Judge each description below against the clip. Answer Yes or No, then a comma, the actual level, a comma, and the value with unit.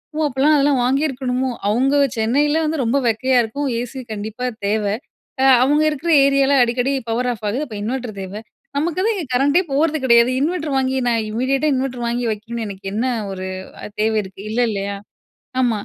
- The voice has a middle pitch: No, very high, 255 Hz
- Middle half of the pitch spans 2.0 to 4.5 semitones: Yes, average, 3.9 semitones